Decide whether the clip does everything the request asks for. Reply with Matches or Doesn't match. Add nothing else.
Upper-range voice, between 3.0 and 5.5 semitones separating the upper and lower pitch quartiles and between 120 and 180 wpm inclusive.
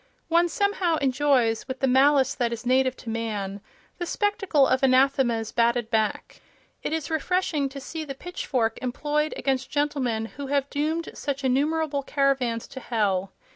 Matches